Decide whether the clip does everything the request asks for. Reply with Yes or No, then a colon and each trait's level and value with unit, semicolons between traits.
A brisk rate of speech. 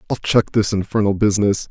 No: average, 175 wpm